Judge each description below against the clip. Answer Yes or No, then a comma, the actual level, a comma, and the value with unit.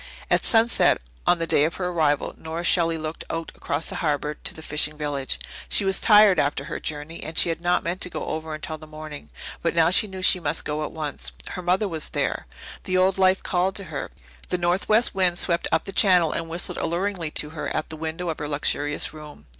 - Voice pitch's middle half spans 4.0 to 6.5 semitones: No, average, 3.0 semitones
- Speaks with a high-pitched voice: No, medium, 165 Hz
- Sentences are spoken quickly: Yes, fast, 230 wpm